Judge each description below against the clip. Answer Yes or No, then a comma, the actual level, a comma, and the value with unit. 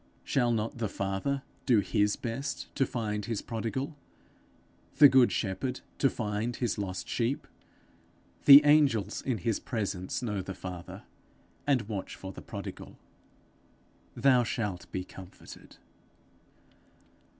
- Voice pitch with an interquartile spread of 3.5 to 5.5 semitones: Yes, average, 4.6 semitones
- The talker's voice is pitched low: Yes, low, 115 Hz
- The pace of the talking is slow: Yes, slow, 125 wpm